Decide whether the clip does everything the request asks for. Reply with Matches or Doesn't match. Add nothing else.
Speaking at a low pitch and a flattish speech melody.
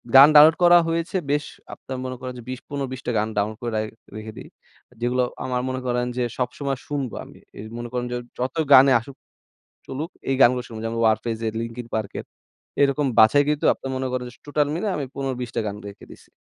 Doesn't match